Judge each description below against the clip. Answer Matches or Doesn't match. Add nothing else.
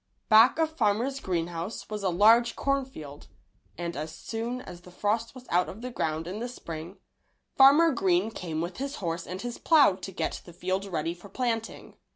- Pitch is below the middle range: Doesn't match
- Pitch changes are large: Matches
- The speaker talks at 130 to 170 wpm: Doesn't match